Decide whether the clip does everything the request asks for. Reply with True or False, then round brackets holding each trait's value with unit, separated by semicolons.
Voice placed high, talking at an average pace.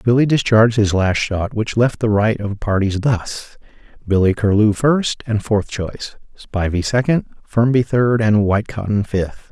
False (110 Hz; 160 wpm)